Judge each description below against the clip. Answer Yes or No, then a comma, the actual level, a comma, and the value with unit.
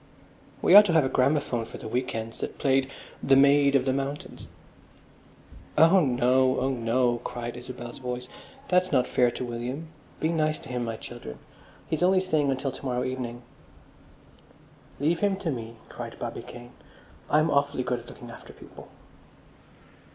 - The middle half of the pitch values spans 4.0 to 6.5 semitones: No, average, 3.3 semitones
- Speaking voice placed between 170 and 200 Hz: No, low, 130 Hz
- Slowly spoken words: No, average, 165 wpm